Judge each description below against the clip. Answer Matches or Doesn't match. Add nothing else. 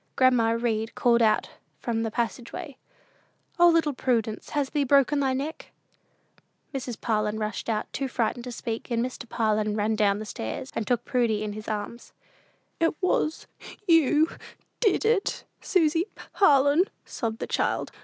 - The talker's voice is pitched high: Matches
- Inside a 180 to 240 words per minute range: Doesn't match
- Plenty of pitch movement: Doesn't match